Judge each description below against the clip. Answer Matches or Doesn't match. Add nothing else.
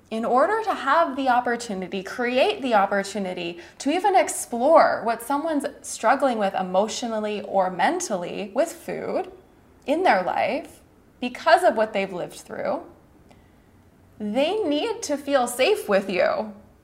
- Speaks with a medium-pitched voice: Doesn't match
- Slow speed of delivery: Matches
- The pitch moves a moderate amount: Doesn't match